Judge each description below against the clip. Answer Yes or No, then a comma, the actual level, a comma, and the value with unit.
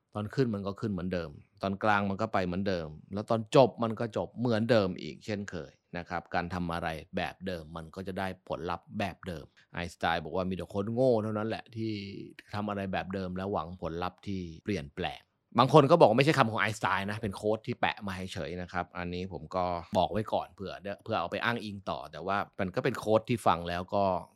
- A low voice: Yes, very low, 95 Hz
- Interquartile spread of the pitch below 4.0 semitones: Yes, average, 3.3 semitones